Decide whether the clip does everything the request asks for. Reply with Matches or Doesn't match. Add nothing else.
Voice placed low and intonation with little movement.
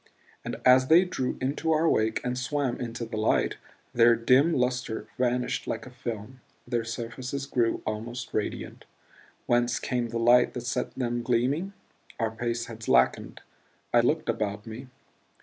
Matches